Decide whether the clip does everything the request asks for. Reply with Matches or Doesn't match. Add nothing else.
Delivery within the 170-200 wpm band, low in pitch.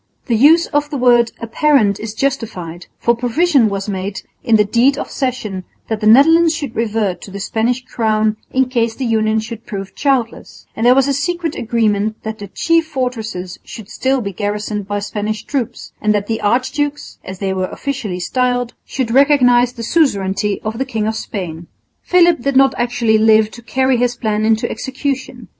Doesn't match